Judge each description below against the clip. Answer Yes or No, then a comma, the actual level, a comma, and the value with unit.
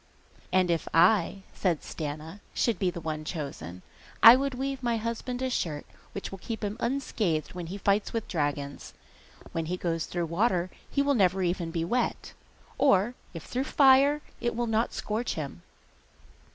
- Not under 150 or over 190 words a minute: Yes, average, 170 wpm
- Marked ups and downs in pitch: Yes, wide, 6.4 semitones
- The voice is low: No, high, 190 Hz